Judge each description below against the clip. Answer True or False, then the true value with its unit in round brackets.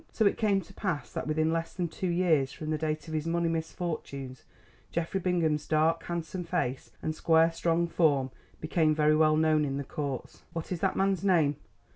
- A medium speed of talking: True (195 wpm)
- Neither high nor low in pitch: True (160 Hz)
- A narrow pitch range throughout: True (2.0 semitones)